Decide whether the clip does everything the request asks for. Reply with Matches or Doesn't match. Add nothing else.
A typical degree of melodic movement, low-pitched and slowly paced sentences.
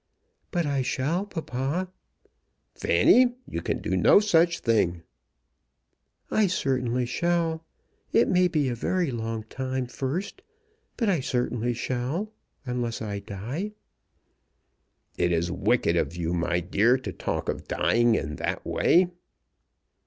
Doesn't match